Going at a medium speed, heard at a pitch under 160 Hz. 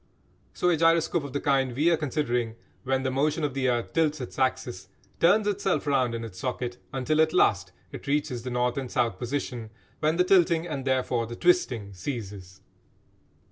Yes: average, 185 wpm; low, 135 Hz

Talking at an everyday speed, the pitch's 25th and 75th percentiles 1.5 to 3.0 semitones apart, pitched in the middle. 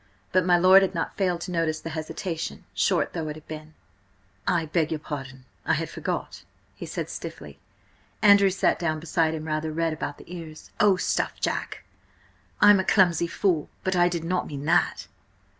Yes: average, 180 wpm; narrow, 2.6 semitones; medium, 165 Hz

